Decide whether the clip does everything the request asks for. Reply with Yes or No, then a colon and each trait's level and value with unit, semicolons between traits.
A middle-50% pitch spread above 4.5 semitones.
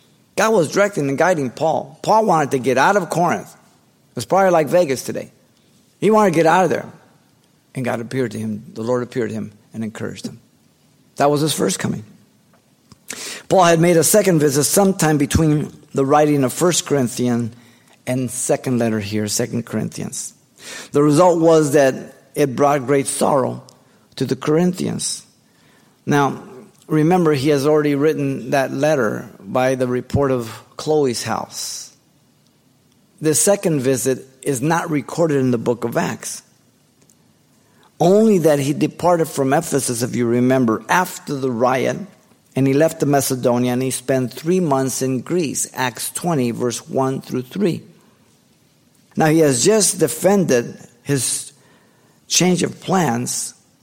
No: average, 4.0 semitones